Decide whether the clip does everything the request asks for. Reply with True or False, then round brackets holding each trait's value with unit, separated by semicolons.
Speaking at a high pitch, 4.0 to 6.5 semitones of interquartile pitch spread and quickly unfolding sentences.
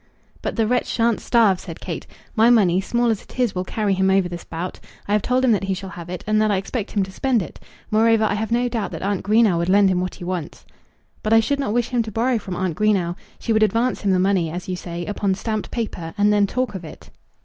False (205 Hz; 3.5 semitones; 270 wpm)